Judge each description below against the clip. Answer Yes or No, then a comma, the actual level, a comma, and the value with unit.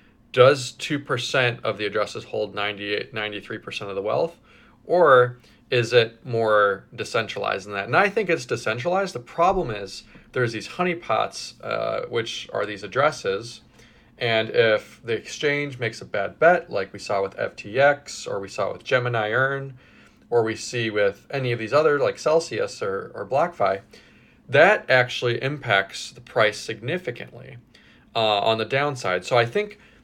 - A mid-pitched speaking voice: No, low, 120 Hz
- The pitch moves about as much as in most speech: Yes, average, 4.9 semitones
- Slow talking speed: No, average, 160 wpm